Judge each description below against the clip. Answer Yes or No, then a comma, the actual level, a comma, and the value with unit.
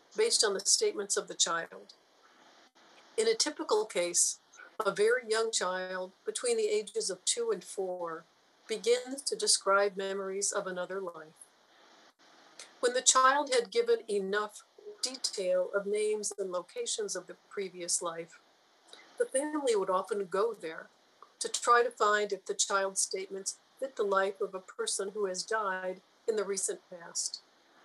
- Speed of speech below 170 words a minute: Yes, average, 155 wpm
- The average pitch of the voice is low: No, high, 225 Hz